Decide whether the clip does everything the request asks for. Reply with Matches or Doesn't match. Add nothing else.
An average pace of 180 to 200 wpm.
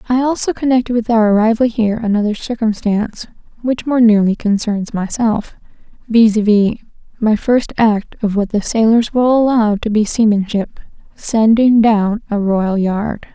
Doesn't match